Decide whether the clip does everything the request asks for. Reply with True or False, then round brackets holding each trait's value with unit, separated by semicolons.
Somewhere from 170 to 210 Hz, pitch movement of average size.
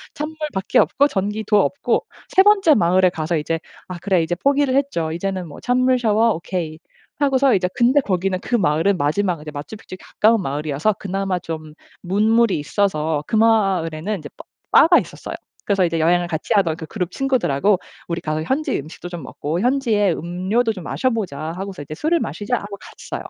False (190 Hz; 5.7 semitones)